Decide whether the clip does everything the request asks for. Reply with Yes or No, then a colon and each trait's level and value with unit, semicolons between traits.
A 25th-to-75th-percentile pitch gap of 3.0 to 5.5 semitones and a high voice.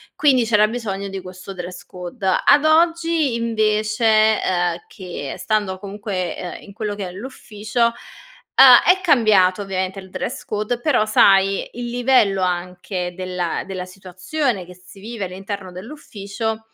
Yes: average, 4.0 semitones; high, 205 Hz